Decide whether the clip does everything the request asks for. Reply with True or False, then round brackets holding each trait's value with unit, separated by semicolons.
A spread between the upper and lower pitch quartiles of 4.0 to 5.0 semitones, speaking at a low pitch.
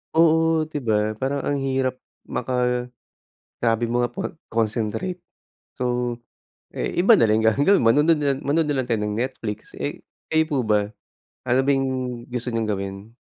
True (4.5 semitones; 125 Hz)